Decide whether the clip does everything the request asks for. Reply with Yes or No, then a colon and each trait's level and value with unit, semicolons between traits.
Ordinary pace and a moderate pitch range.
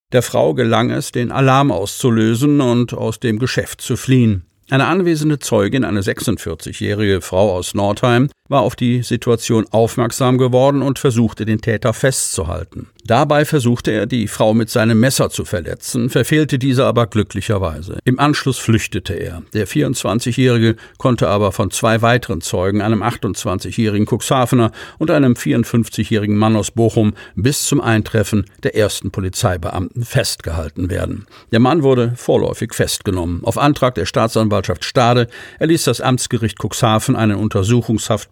Yes: average, 140 wpm; average, 3.2 semitones